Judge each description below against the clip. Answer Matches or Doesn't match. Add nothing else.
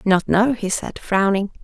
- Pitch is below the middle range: Doesn't match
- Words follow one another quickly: Doesn't match